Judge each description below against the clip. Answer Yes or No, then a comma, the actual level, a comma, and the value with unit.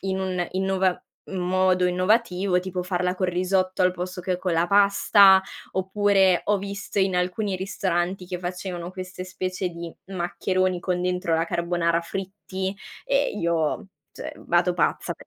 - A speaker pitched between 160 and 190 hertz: Yes, medium, 185 Hz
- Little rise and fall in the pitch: Yes, narrow, 1.2 semitones